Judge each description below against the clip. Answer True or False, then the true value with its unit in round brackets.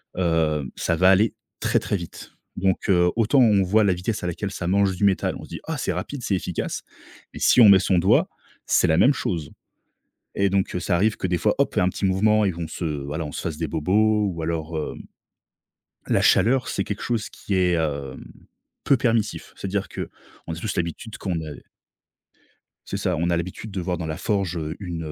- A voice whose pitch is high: False (90 Hz)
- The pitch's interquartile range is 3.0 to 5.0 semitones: True (3.6 semitones)